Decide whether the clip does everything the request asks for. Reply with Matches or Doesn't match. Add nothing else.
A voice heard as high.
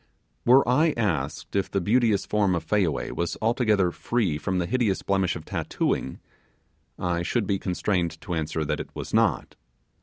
Doesn't match